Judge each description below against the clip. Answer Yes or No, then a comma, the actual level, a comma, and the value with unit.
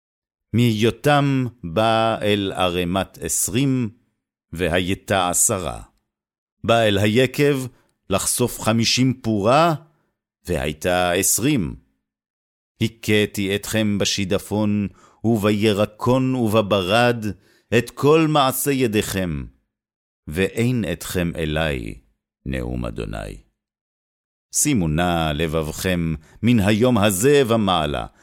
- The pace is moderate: No, slow, 80 wpm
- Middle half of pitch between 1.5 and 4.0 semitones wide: No, average, 5.0 semitones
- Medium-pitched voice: No, low, 105 Hz